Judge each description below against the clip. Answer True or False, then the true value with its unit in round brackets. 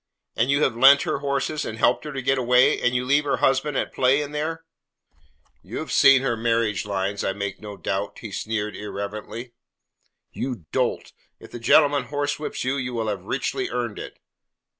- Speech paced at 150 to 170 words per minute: False (190 wpm)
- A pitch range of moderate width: True (4.5 semitones)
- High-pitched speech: False (125 Hz)